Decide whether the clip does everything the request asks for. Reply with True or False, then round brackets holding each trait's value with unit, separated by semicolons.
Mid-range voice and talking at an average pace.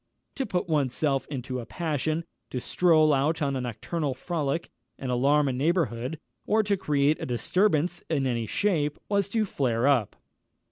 True (150 Hz; 170 wpm)